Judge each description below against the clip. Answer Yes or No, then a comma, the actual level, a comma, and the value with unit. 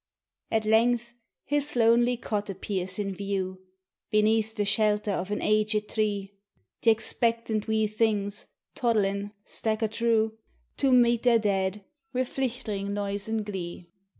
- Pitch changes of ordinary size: No, narrow, 2.2 semitones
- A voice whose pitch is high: Yes, high, 215 Hz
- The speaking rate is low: Yes, slow, 130 wpm